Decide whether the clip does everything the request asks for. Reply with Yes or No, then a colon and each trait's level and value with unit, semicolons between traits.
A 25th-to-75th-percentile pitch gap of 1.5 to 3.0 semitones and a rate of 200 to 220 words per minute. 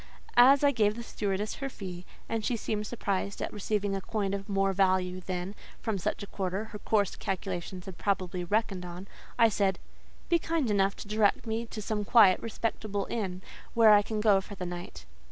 No: narrow, 2.5 semitones; average, 190 wpm